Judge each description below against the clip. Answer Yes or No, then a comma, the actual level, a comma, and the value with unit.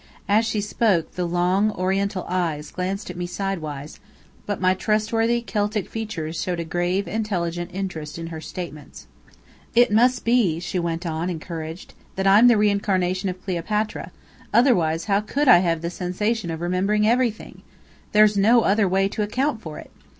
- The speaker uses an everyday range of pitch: Yes, average, 3.6 semitones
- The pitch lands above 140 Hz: Yes, high, 190 Hz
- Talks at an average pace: Yes, average, 165 wpm